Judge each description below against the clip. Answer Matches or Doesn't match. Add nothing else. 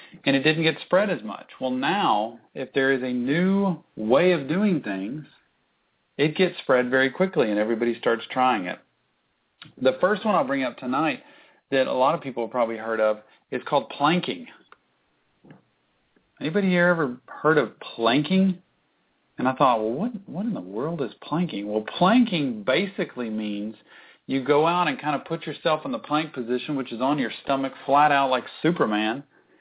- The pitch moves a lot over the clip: Matches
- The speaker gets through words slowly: Doesn't match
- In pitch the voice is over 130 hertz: Matches